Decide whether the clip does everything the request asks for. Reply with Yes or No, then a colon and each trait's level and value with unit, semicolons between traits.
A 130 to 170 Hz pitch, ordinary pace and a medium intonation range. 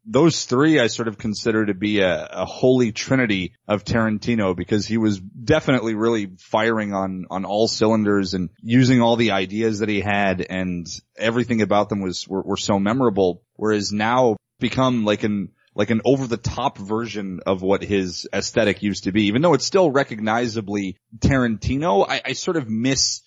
No: low, 110 Hz; average, 180 wpm; average, 3.2 semitones